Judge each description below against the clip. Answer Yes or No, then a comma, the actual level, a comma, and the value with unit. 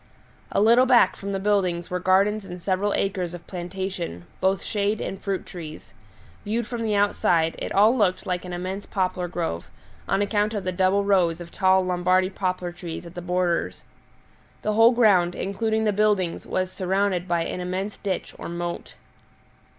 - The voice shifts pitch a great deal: No, narrow, 2.4 semitones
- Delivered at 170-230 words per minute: Yes, average, 175 wpm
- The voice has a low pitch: No, medium, 185 Hz